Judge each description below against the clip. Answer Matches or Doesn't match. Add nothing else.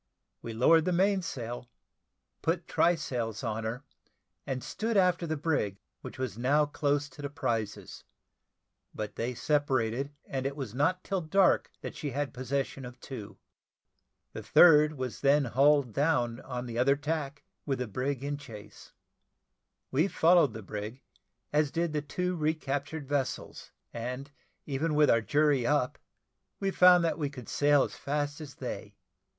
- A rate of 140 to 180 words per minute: Matches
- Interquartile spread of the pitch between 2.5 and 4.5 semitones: Matches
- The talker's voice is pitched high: Doesn't match